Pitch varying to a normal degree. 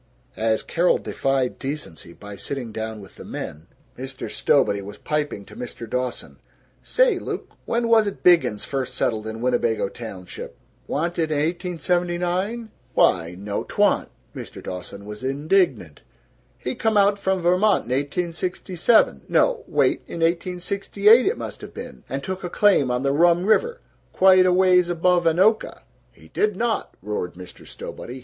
No: wide, 8.3 semitones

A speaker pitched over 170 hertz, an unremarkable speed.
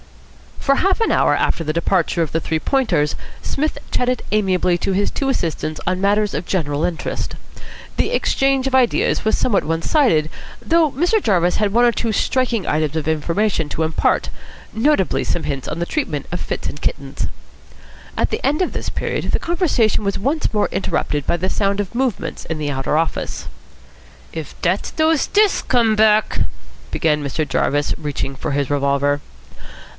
Yes: high, 190 Hz; average, 180 wpm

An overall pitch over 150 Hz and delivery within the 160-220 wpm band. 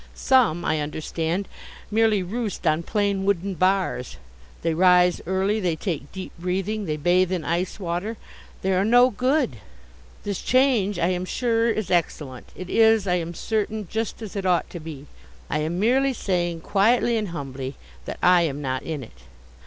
Yes: medium, 185 Hz; average, 170 wpm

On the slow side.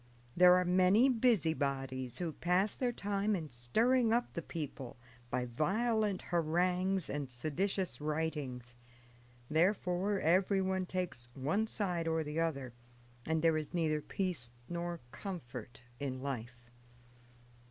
Yes: slow, 120 wpm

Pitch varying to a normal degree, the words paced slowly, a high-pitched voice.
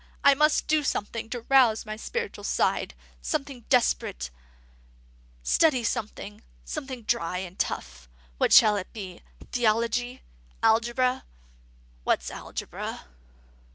Yes: average, 3.8 semitones; slow, 110 wpm; high, 230 Hz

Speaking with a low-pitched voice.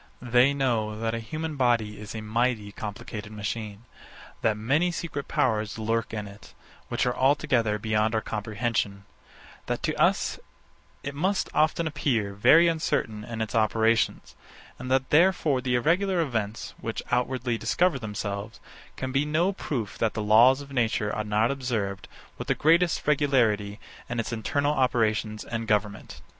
Yes: low, 115 Hz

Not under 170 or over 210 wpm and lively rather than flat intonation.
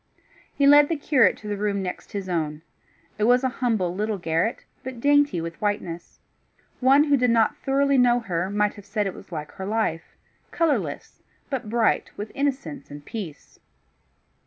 Yes: average, 175 wpm; wide, 6.1 semitones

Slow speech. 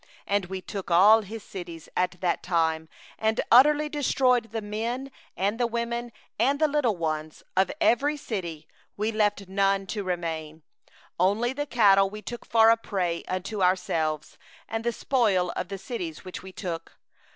No: average, 160 wpm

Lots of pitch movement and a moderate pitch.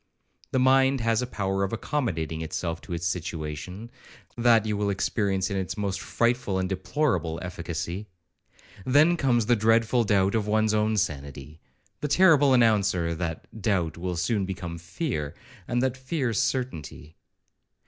No: wide, 5.7 semitones; low, 100 Hz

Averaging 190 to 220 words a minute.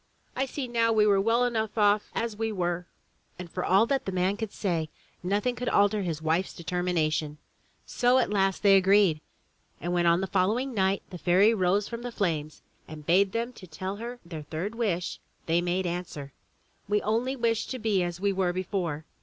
Yes: average, 195 wpm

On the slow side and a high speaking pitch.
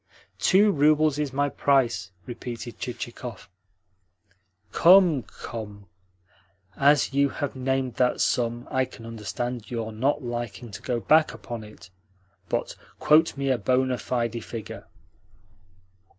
No: slow, 120 wpm; low, 125 Hz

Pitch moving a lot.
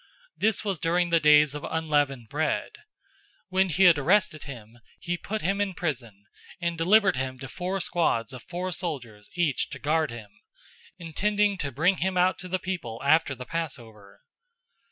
Yes: wide, 5.7 semitones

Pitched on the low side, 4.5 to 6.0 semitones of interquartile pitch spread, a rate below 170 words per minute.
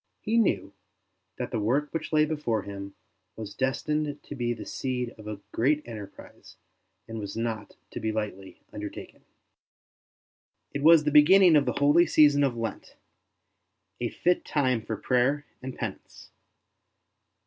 Yes: low, 130 Hz; average, 5.1 semitones; average, 150 wpm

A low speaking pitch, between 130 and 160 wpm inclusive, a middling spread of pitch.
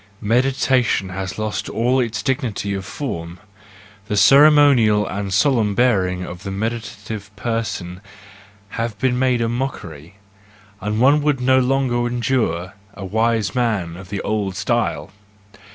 Yes: low, 110 Hz; slow, 135 wpm; average, 4.5 semitones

